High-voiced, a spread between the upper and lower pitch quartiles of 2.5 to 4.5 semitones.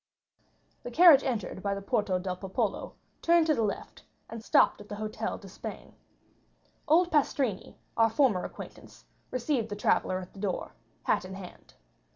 No: high, 215 Hz; wide, 5.4 semitones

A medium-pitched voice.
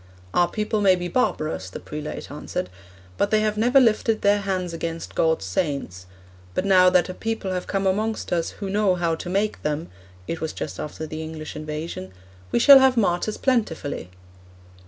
Yes: medium, 180 Hz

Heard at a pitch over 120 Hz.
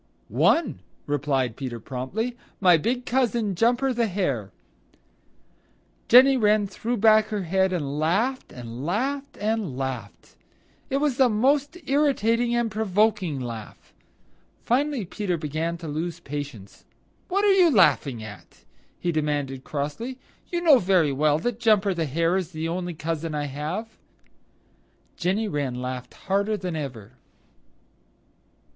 Yes: medium, 185 Hz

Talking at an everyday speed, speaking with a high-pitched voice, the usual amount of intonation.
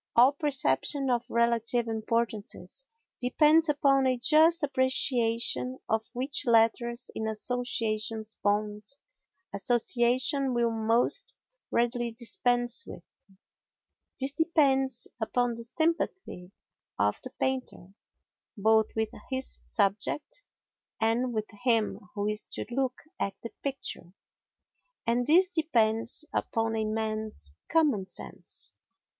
No: slow, 105 wpm; high, 240 Hz; average, 3.3 semitones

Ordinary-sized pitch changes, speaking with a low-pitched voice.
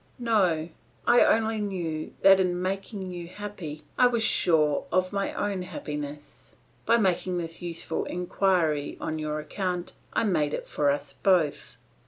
No: average, 4.1 semitones; medium, 180 Hz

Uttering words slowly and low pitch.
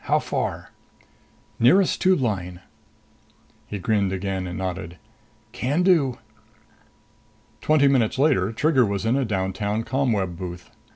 Yes: slow, 120 wpm; low, 110 Hz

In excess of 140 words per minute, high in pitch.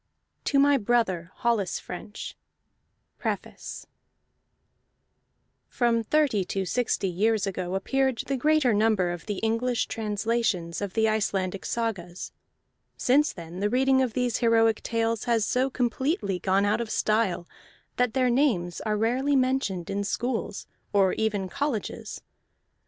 No: slow, 135 wpm; high, 225 Hz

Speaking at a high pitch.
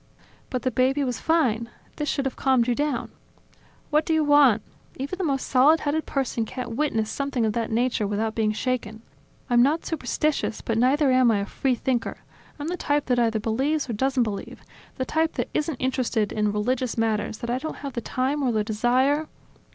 Yes: very high, 255 Hz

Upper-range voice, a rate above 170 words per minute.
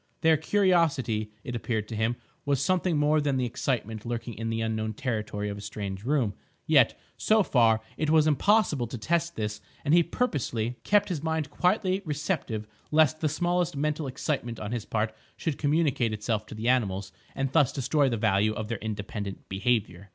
No: low, 125 Hz; average, 180 wpm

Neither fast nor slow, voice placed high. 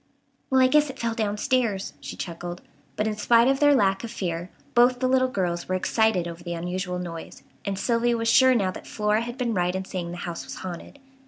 No: fast, 225 wpm; high, 210 Hz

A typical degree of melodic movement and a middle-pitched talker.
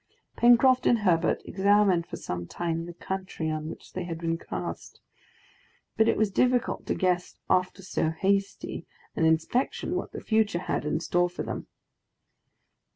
Yes: average, 3.8 semitones; medium, 180 Hz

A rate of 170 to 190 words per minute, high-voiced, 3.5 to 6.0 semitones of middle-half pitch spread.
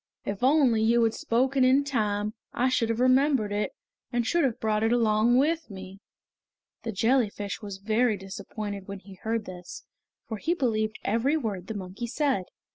Yes: average, 175 wpm; high, 225 Hz; average, 3.8 semitones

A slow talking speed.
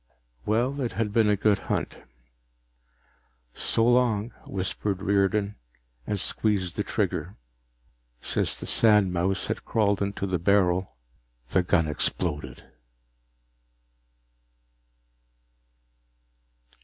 Yes: slow, 95 wpm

